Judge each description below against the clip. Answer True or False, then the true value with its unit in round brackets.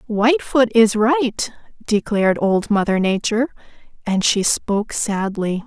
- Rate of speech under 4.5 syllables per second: True (4.2 syllables/s)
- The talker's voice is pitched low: False (220 Hz)